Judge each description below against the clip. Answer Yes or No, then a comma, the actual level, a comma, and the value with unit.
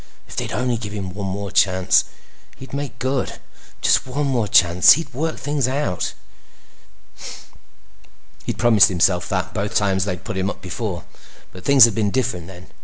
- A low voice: Yes, low, 105 Hz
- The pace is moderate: Yes, average, 170 wpm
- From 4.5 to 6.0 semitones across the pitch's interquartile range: Yes, wide, 5.6 semitones